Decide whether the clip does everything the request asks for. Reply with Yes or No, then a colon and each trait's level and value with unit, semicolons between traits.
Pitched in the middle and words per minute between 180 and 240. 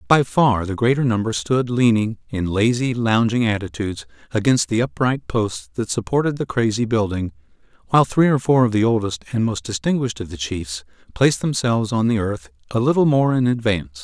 No: low, 115 Hz; average, 185 wpm